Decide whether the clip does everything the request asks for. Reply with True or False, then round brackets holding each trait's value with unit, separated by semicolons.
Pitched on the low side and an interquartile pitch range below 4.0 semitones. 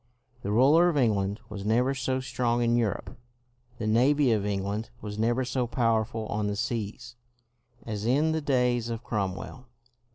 True (115 Hz; 3.2 semitones)